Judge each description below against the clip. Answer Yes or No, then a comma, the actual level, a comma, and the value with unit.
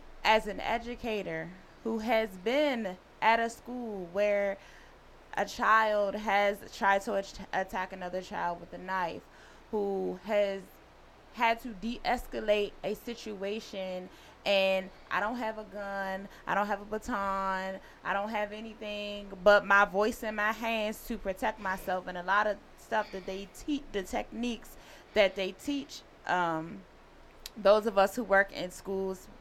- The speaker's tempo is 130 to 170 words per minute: Yes, average, 150 wpm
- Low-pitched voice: No, high, 205 Hz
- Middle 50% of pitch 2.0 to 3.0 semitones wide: Yes, narrow, 2.4 semitones